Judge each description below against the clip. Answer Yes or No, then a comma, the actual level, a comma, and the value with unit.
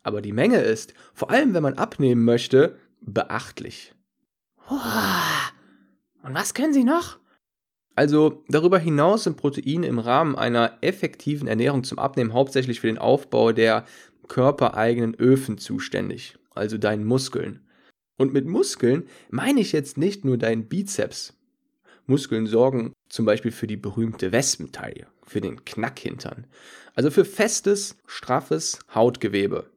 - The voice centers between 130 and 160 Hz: Yes, low, 135 Hz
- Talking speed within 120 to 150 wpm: Yes, average, 130 wpm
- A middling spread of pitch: No, wide, 7.9 semitones